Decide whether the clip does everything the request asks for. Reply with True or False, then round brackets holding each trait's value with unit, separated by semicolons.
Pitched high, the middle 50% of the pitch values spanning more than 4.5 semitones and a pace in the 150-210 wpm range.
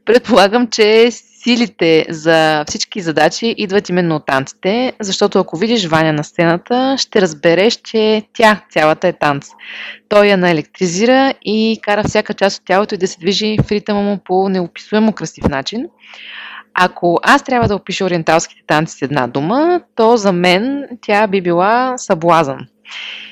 True (200 Hz; 4.9 semitones; 155 wpm)